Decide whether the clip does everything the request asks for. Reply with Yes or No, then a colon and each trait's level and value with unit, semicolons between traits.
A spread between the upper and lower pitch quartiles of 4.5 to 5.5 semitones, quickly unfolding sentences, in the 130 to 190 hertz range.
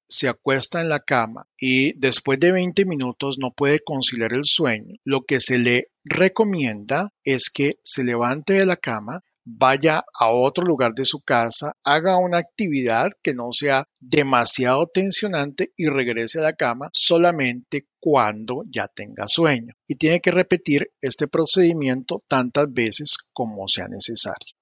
No: average, 4.9 semitones; average, 155 wpm; medium, 140 Hz